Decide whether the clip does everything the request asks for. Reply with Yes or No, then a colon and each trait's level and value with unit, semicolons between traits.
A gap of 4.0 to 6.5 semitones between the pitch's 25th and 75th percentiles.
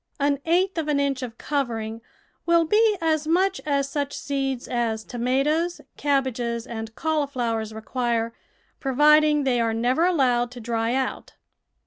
Yes: average, 4.4 semitones